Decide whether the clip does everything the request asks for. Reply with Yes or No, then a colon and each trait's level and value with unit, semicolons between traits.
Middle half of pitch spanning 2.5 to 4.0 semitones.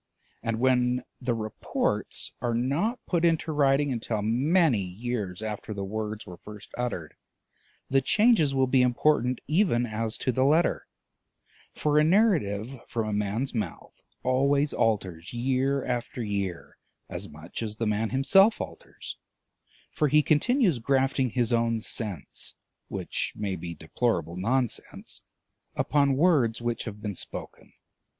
No: average, 4.6 semitones